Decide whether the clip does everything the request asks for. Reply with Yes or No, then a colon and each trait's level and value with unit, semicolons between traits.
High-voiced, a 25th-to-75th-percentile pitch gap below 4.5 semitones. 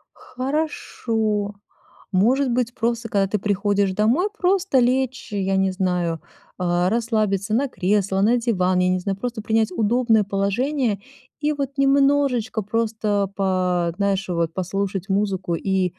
Yes: high, 210 Hz; average, 4.1 semitones